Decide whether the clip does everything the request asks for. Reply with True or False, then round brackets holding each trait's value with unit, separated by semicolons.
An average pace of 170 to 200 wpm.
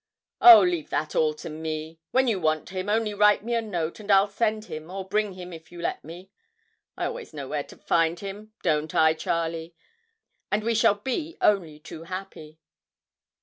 True (190 wpm)